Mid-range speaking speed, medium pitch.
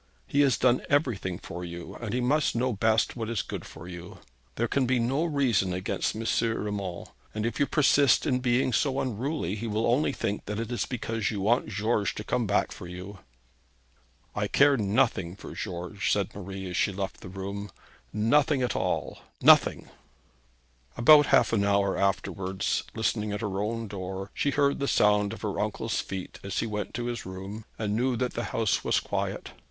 No: average, 190 wpm; low, 110 Hz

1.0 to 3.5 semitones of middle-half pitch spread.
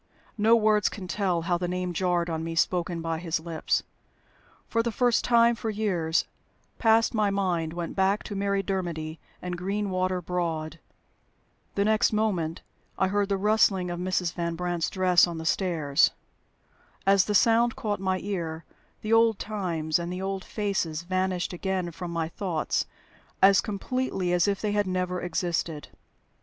Yes: average, 3.1 semitones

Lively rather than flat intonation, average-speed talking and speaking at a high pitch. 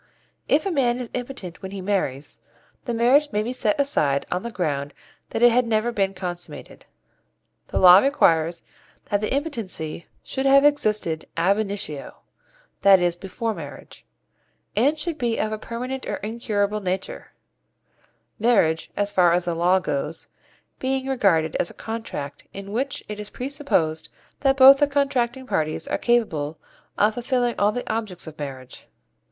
Yes: wide, 6.2 semitones; average, 160 wpm; high, 210 Hz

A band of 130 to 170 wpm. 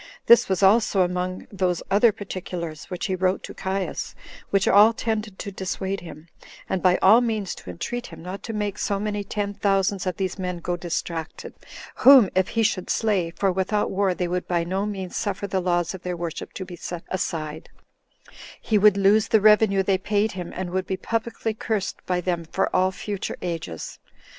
No: average, 195 wpm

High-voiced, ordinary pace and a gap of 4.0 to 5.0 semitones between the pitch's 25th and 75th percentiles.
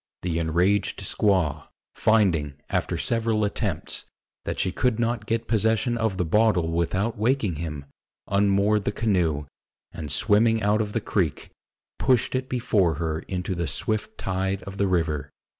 No: low, 100 Hz; average, 150 wpm; average, 4.5 semitones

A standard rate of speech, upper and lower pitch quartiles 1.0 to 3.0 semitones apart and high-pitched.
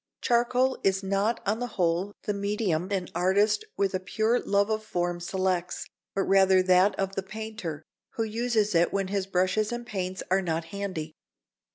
Yes: average, 175 wpm; average, 2.7 semitones; high, 195 Hz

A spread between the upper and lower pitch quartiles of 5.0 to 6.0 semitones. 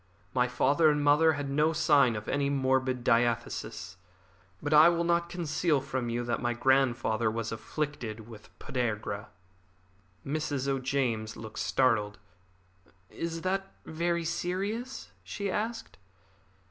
Yes: wide, 5.4 semitones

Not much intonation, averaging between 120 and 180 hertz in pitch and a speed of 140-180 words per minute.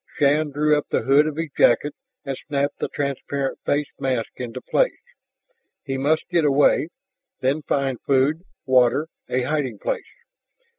Yes: narrow, 2.2 semitones; medium, 140 Hz; average, 150 wpm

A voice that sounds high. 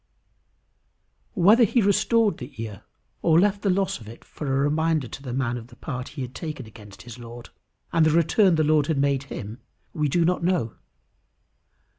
No: medium, 150 Hz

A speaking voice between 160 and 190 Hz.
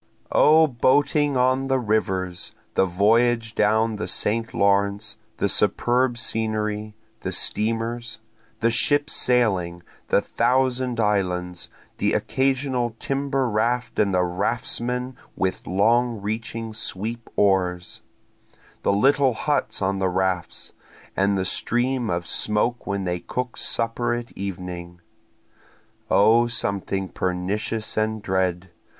No: low, 110 Hz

